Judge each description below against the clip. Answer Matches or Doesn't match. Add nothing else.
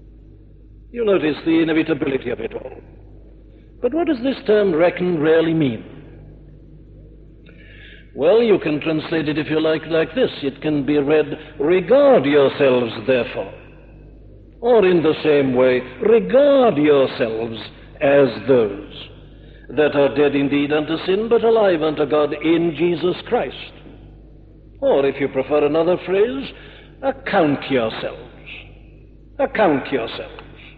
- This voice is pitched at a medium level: Matches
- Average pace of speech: Doesn't match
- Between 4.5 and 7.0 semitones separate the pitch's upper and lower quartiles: Matches